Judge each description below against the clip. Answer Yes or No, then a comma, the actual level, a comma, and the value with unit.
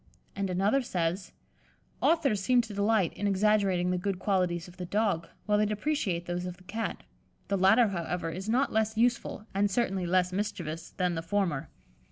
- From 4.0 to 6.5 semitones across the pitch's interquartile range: No, average, 3.0 semitones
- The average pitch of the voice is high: Yes, high, 195 Hz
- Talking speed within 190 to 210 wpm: No, average, 180 wpm